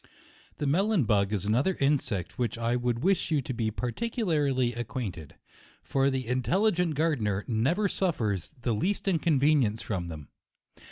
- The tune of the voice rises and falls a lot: Yes, wide, 6.7 semitones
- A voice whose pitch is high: No, low, 130 Hz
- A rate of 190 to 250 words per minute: No, average, 160 wpm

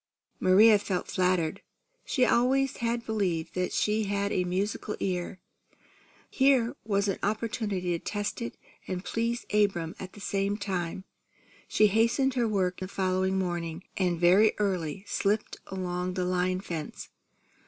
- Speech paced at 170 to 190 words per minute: No, average, 145 wpm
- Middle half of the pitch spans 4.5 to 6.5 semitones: No, average, 3.0 semitones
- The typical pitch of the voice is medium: No, high, 195 Hz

